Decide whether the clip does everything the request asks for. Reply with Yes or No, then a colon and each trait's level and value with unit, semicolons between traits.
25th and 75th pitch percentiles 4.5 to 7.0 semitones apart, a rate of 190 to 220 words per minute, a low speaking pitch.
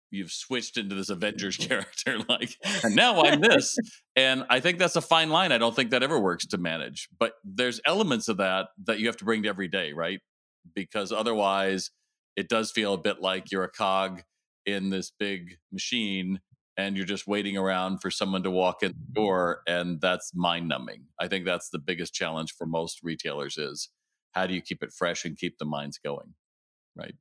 No: average, 3.6 semitones; fast, 205 wpm; very low, 95 Hz